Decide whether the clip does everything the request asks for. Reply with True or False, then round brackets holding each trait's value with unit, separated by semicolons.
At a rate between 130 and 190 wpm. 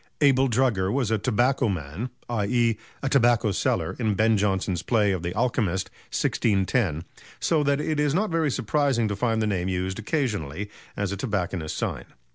True (170 wpm)